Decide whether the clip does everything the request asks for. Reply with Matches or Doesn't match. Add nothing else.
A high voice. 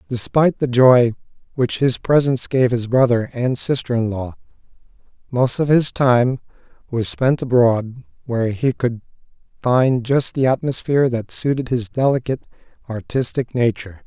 Doesn't match